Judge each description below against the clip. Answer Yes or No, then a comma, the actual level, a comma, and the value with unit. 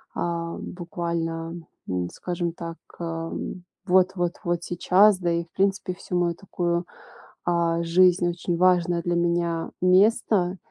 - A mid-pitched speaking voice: Yes, medium, 175 Hz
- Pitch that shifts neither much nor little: No, narrow, 1.3 semitones